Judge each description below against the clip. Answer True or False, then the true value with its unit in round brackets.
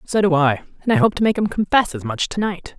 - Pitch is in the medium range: False (200 Hz)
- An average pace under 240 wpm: False (300 wpm)